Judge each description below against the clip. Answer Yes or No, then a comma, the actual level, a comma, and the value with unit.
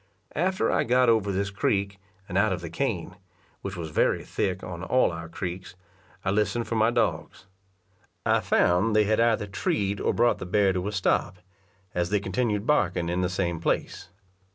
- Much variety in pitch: No, average, 3.3 semitones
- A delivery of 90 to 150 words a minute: No, average, 185 wpm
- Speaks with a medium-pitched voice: No, low, 100 Hz